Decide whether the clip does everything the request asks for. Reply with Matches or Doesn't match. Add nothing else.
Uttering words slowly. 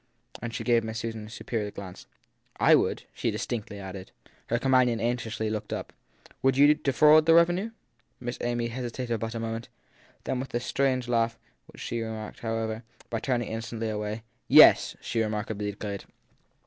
Doesn't match